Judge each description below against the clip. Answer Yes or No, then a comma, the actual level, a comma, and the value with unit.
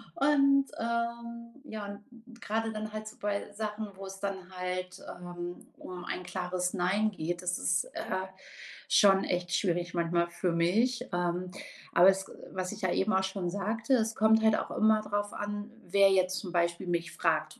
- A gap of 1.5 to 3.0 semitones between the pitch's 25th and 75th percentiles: No, average, 3.4 semitones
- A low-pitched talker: No, high, 195 Hz